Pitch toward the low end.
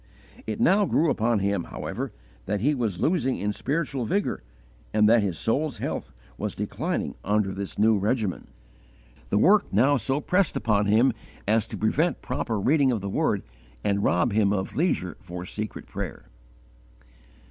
Yes: low, 110 Hz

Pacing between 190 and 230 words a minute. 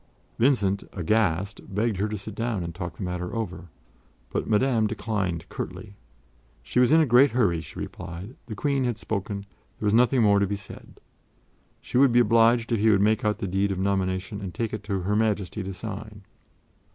Yes: average, 200 wpm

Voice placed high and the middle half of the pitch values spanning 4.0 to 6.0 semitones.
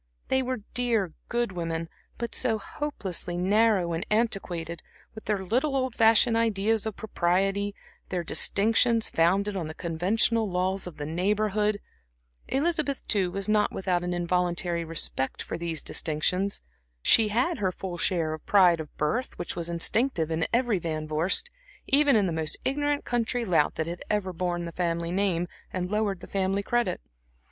Yes: high, 195 Hz; average, 4.6 semitones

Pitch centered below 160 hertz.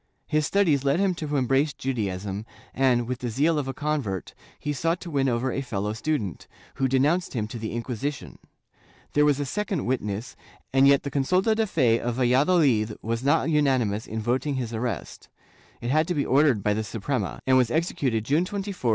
Yes: low, 135 Hz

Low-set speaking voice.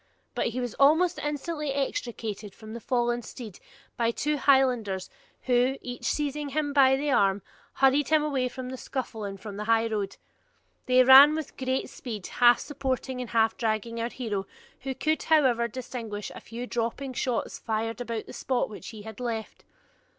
No: high, 245 Hz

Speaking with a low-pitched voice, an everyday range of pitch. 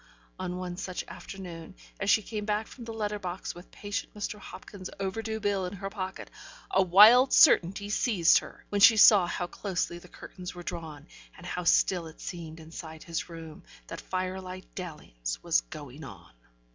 No: medium, 185 Hz; average, 3.5 semitones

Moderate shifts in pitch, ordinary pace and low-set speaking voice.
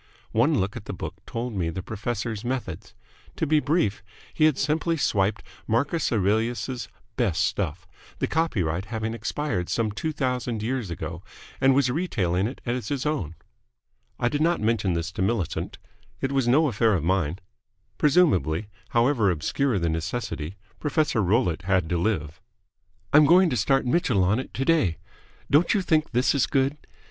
No: wide, 6.8 semitones; average, 165 wpm; low, 115 Hz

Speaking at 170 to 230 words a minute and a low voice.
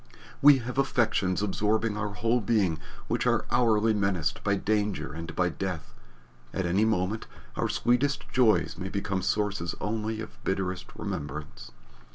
No: average, 145 wpm; low, 105 Hz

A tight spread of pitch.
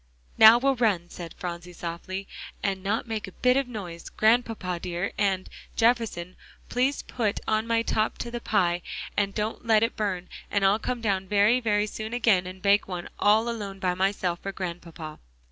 No: average, 3.7 semitones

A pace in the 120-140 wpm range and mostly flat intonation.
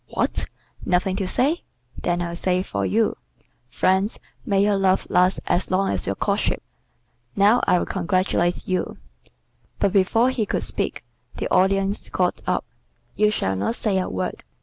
No: average, 160 wpm; narrow, 2.2 semitones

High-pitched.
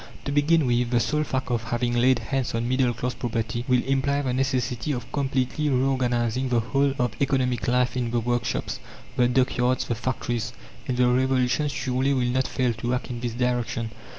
No: low, 125 Hz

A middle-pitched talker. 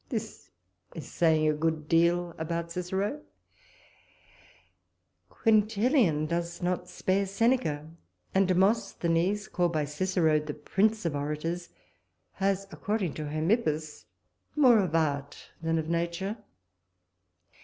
Yes: medium, 170 Hz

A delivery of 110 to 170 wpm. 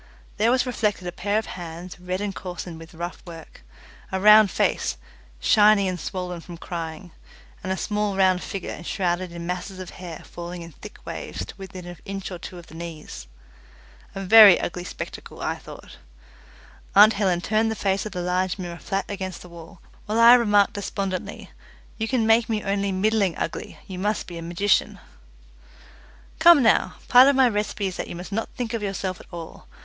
No: average, 190 wpm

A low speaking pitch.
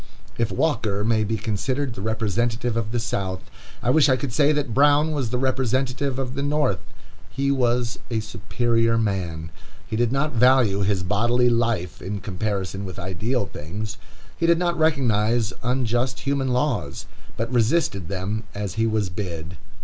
Yes: low, 115 Hz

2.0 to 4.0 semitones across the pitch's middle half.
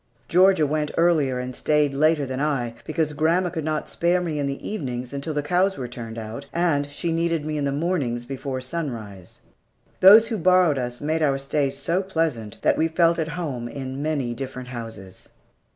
No: average, 4.4 semitones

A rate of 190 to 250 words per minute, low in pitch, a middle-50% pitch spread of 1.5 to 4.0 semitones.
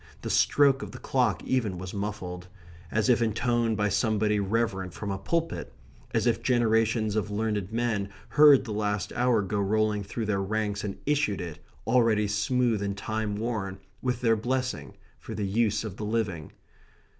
No: average, 170 wpm; low, 110 Hz; narrow, 2.6 semitones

